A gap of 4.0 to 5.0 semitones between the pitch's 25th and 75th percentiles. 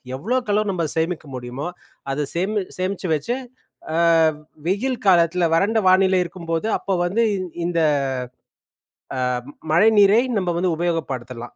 No: average, 3.6 semitones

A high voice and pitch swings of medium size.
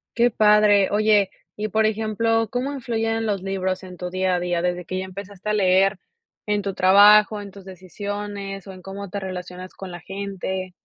No: high, 195 Hz; narrow, 2.2 semitones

